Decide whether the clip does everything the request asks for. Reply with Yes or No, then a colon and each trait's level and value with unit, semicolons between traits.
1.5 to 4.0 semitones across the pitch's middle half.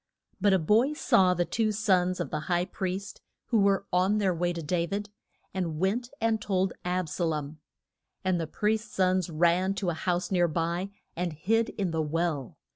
Yes: average, 2.8 semitones